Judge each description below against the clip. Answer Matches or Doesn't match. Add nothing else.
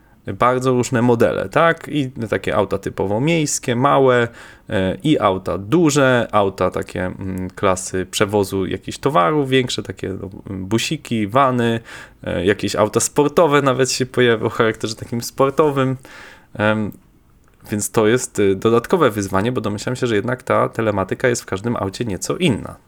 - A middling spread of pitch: Matches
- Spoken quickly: Doesn't match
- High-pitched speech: Doesn't match